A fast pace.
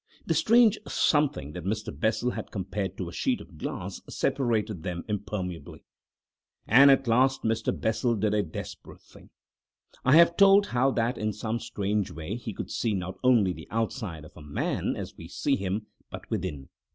No: average, 175 wpm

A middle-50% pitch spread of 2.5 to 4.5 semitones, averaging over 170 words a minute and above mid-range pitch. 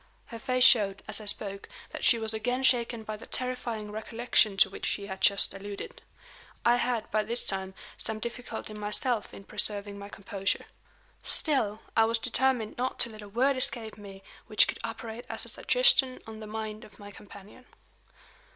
Yes: average, 2.9 semitones; average, 180 wpm; high, 220 Hz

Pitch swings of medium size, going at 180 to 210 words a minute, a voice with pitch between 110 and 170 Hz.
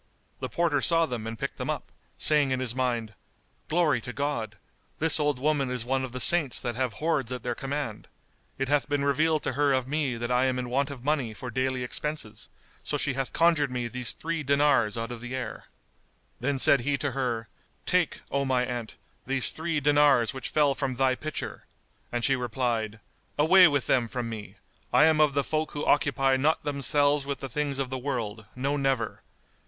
Yes: average, 3.0 semitones; fast, 205 wpm; low, 135 Hz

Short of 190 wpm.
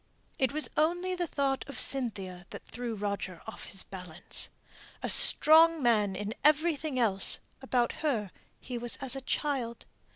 Yes: average, 155 wpm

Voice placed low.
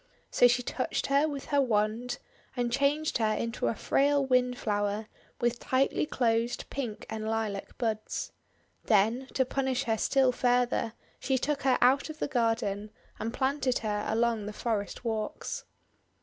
No: high, 245 Hz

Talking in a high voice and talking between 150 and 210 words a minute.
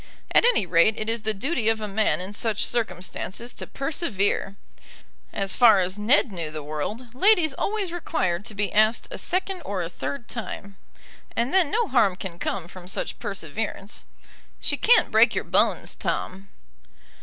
Yes: high, 215 Hz; average, 170 wpm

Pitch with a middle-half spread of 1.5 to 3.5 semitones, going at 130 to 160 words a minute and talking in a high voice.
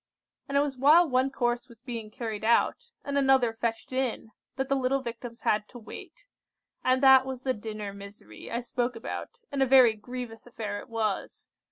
No: average, 3.0 semitones; average, 190 wpm; high, 245 Hz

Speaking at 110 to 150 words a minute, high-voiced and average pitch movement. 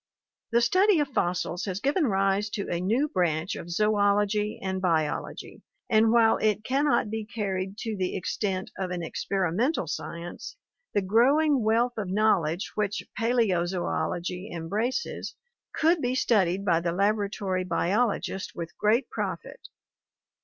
Yes: average, 140 wpm; high, 205 Hz; average, 3.9 semitones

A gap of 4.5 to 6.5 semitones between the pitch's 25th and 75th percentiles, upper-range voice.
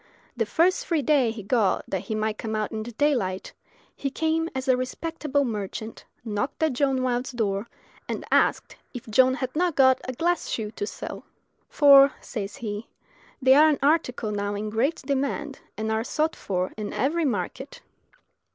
Yes: average, 4.9 semitones; very high, 255 Hz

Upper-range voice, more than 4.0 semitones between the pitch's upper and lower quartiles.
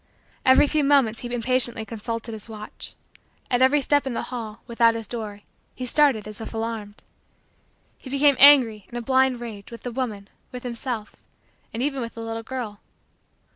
No: high, 235 Hz; average, 2.8 semitones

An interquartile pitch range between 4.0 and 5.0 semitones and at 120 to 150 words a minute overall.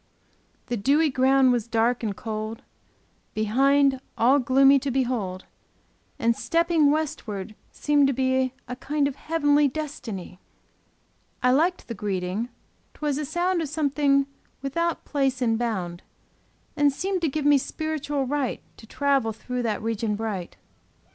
Yes: average, 4.4 semitones; average, 140 wpm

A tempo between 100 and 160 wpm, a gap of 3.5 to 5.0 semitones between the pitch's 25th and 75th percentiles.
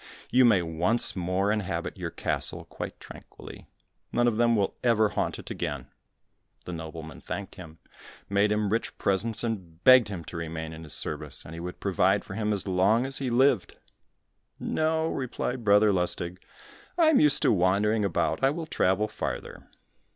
No: average, 175 wpm; average, 4.7 semitones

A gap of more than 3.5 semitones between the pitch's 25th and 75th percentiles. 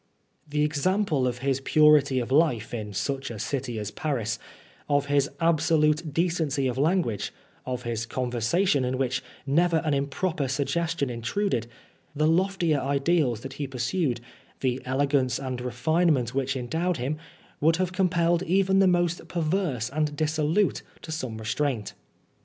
Yes: average, 4.7 semitones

